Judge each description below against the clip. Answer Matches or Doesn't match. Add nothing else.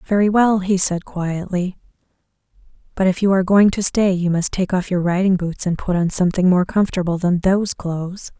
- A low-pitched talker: Doesn't match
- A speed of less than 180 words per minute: Doesn't match